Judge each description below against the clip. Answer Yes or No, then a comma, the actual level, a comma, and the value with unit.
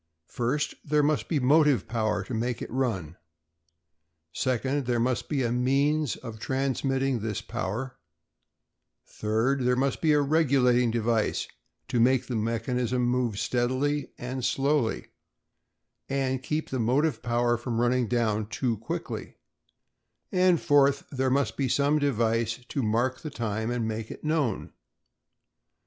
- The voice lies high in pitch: No, low, 125 Hz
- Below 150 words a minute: Yes, average, 140 wpm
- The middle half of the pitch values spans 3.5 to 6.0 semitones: No, average, 3.1 semitones